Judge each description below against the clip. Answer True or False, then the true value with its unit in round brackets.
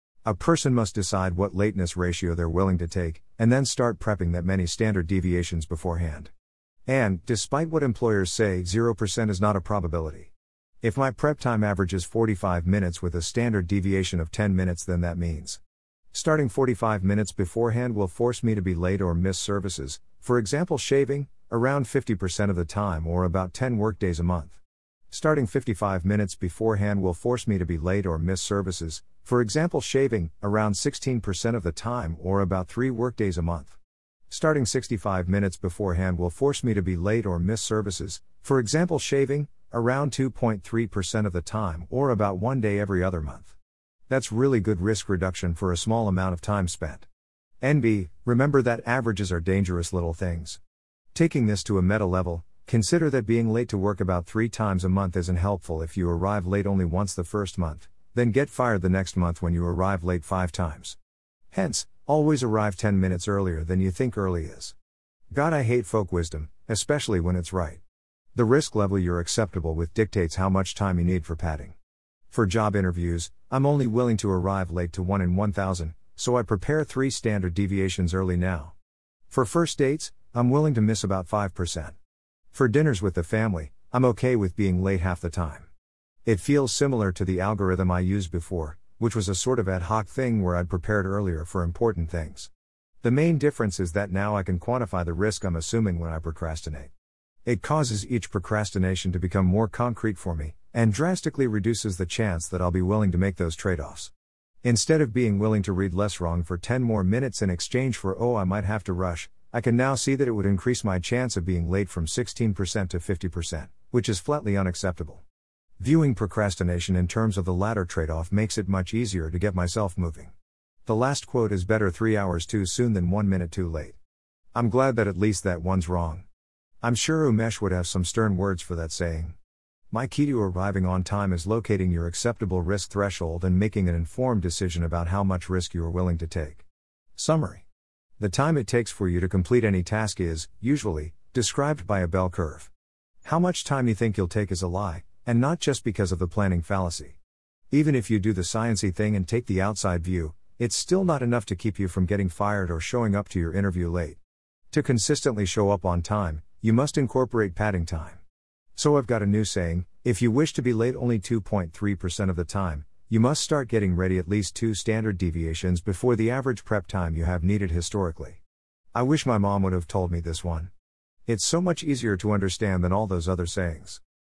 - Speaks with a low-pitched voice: True (95 Hz)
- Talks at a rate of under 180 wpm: False (200 wpm)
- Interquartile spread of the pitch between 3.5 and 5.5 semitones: True (4.4 semitones)